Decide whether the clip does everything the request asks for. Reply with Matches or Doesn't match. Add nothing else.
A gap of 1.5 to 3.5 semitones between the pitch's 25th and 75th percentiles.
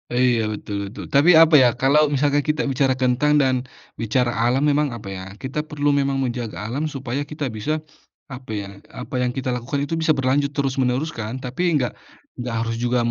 Matches